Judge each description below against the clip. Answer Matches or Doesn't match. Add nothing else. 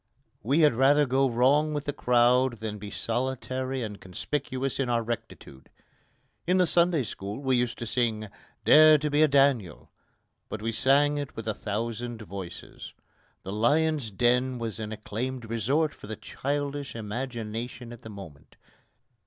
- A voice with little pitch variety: Doesn't match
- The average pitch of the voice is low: Matches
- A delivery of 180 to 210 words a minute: Doesn't match